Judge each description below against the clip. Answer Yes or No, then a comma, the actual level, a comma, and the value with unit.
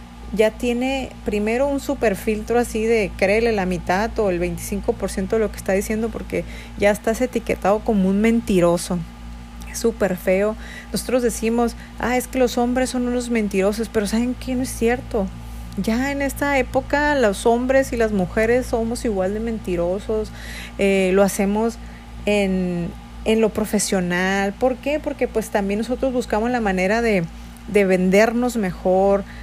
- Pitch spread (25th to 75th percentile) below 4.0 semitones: Yes, average, 3.5 semitones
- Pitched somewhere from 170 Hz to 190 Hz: No, high, 220 Hz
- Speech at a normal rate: Yes, average, 160 wpm